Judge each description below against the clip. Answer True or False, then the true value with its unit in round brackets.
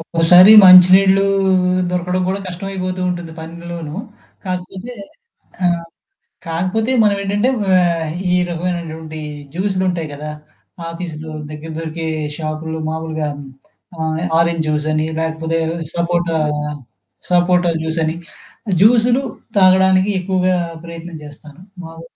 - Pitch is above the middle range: False (170 Hz)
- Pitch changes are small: True (2.3 semitones)